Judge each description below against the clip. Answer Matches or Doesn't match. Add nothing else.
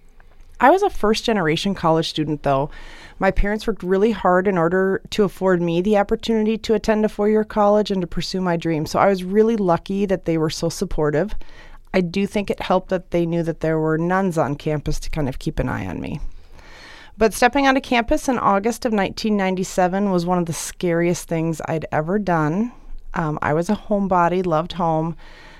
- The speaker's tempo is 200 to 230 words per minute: Matches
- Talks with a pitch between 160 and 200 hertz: Matches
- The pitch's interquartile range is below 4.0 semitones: Doesn't match